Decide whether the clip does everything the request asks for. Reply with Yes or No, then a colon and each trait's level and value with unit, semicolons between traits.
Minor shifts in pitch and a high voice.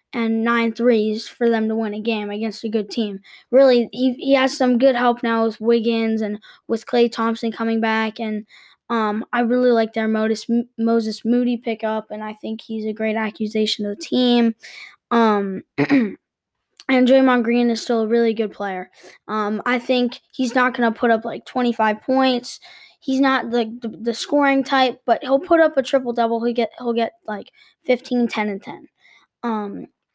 Yes: narrow, 2.2 semitones; high, 230 Hz